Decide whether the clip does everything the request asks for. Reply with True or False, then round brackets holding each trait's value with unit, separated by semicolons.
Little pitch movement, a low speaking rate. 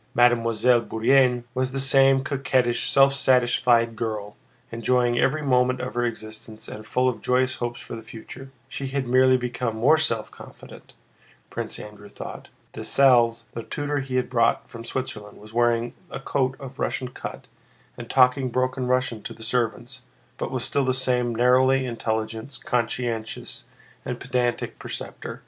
False (2.0 semitones; 155 wpm)